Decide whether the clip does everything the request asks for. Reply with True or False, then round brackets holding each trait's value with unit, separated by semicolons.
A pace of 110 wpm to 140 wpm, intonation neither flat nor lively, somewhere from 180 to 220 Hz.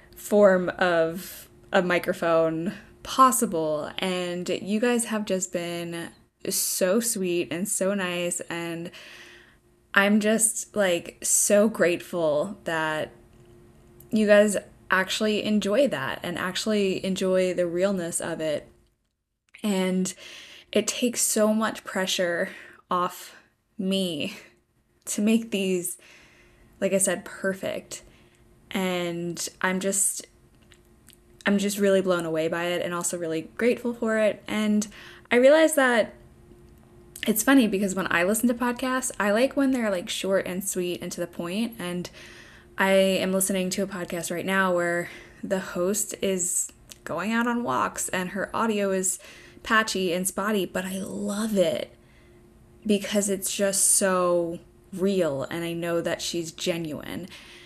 True (135 wpm; 3.1 semitones; 190 Hz)